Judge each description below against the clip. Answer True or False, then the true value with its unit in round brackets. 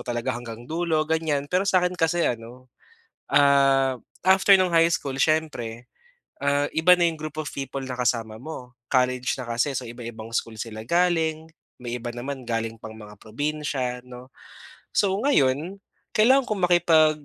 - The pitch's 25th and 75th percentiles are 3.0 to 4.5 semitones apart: False (5.0 semitones)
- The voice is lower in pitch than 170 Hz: True (140 Hz)